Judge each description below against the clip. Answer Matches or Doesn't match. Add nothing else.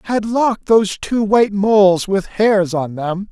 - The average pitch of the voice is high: Matches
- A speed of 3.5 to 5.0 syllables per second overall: Matches